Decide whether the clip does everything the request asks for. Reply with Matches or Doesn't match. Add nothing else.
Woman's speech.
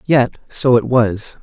Doesn't match